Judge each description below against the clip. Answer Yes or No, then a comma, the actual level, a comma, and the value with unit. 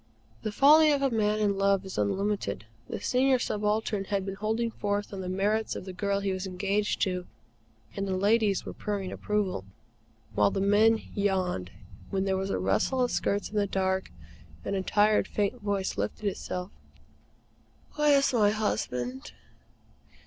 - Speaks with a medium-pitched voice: No, high, 200 Hz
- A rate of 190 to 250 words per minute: No, average, 165 wpm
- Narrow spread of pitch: Yes, narrow, 2.1 semitones